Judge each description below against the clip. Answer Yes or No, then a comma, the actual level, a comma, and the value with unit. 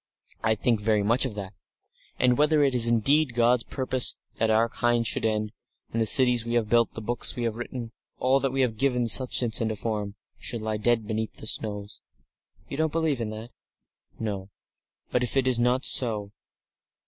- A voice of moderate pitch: No, low, 115 Hz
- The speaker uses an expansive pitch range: No, narrow, 2.5 semitones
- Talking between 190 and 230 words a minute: Yes, average, 195 wpm